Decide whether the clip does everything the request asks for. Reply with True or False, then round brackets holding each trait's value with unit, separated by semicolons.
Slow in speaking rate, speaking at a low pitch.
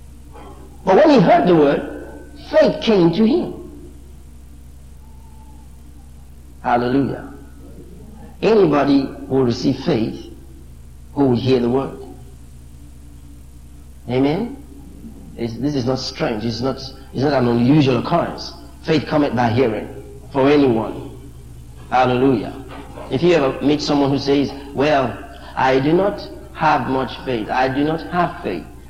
True (125 wpm; 115 Hz)